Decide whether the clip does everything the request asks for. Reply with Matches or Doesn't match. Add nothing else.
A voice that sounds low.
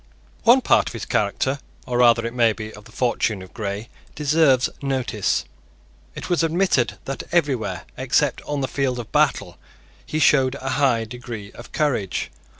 Matches